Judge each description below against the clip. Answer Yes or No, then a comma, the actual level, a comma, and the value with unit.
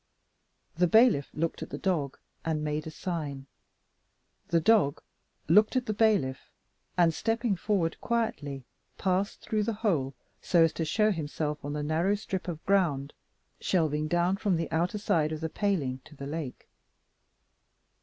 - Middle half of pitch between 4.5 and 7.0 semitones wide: Yes, average, 5.0 semitones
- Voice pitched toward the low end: No, medium, 165 Hz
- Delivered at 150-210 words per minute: Yes, average, 155 wpm